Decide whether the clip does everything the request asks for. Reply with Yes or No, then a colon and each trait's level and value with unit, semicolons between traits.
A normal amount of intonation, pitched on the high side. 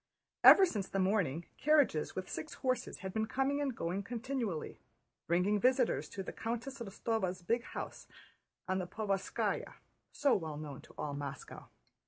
No: wide, 5.8 semitones; high, 200 Hz